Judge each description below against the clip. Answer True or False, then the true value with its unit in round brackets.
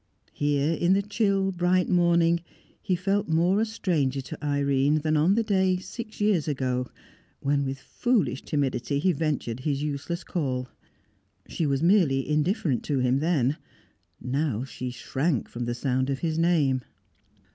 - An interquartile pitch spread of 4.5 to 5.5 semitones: True (5.1 semitones)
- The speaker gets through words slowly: False (155 wpm)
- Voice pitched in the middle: True (150 Hz)